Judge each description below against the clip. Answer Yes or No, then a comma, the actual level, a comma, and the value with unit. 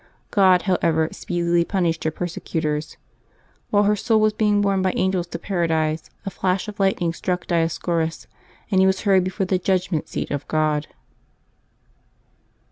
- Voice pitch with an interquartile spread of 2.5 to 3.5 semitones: Yes, average, 2.8 semitones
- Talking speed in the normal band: Yes, average, 150 wpm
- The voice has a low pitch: No, medium, 180 Hz